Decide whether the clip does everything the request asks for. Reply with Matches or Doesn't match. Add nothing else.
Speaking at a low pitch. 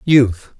Matches